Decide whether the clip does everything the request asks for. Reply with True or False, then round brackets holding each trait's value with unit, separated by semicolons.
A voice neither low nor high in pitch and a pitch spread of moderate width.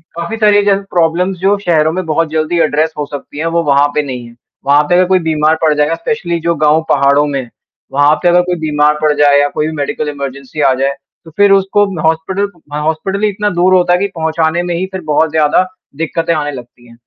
True (160 Hz; 3.3 semitones)